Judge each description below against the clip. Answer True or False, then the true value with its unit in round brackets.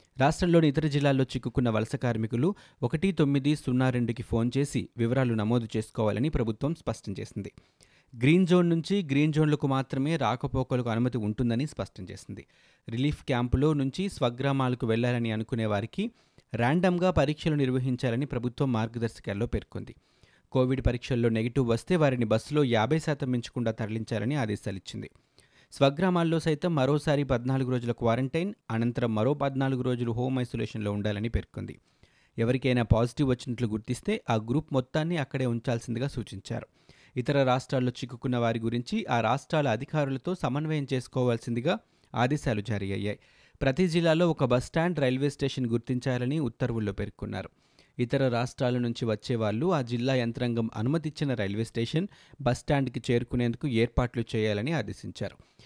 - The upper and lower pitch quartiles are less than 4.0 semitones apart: True (3.5 semitones)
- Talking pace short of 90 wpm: False (125 wpm)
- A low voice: True (125 Hz)